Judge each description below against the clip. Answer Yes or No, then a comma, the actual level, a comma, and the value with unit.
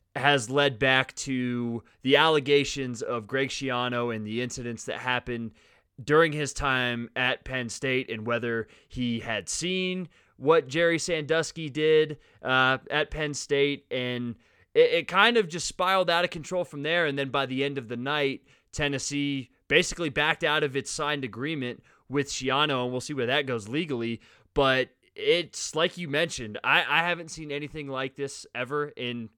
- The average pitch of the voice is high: No, medium, 140 Hz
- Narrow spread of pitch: No, average, 3.8 semitones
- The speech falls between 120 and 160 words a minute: No, average, 170 wpm